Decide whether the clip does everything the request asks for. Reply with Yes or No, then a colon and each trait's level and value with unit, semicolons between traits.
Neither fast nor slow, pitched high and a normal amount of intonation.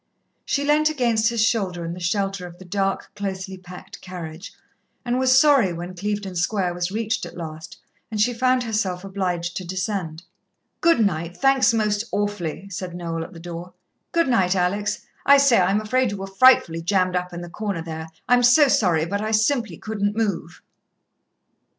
Yes: average, 180 wpm; high, 195 Hz; average, 4.0 semitones